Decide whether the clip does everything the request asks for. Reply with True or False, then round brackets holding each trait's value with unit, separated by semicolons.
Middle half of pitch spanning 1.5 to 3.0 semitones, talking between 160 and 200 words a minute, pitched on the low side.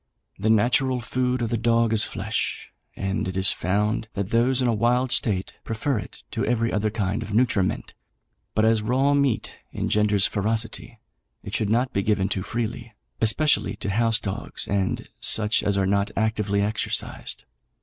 True (2.7 semitones; 170 wpm; 110 Hz)